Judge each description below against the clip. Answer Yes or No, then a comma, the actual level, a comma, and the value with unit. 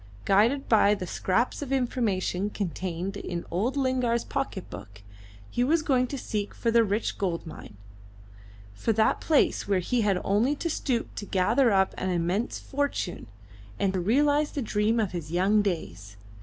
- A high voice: Yes, high, 210 Hz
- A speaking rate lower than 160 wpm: No, average, 165 wpm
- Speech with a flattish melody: No, average, 5.3 semitones